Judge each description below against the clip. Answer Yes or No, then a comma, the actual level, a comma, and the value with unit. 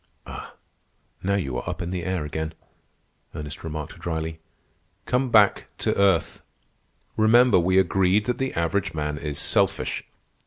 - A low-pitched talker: Yes, very low, 90 Hz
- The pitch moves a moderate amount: Yes, average, 4.1 semitones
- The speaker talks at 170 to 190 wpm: No, average, 145 wpm